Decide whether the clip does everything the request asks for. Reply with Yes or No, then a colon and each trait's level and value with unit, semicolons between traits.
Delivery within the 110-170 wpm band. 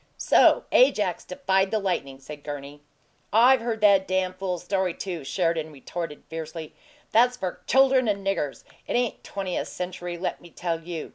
Yes: average, 160 wpm